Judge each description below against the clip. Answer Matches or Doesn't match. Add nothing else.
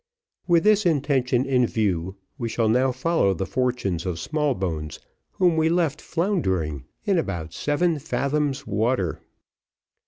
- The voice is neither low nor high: Doesn't match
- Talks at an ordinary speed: Doesn't match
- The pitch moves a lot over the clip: Matches